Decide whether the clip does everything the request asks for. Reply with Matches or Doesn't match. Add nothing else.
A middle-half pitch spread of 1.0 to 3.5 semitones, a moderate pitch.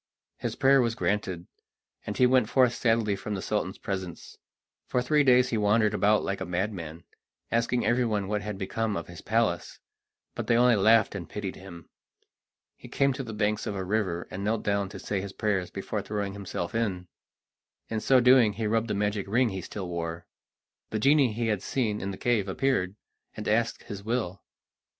Doesn't match